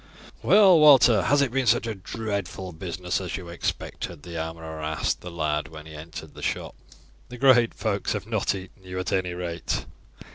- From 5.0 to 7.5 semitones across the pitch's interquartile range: Yes, wide, 5.4 semitones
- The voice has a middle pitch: No, very low, 95 Hz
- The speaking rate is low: No, average, 190 wpm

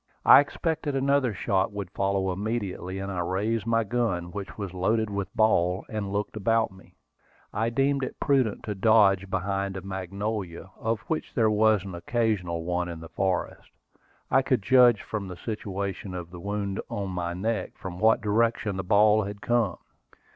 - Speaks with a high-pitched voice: No, low, 100 Hz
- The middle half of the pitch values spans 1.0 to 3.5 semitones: Yes, average, 3.1 semitones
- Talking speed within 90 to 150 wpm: No, average, 175 wpm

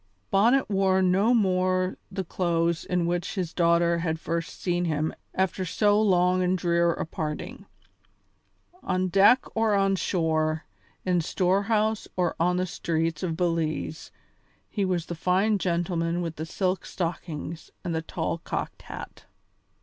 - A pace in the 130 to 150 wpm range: Yes, average, 145 wpm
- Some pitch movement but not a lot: No, narrow, 2.2 semitones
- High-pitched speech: No, medium, 180 Hz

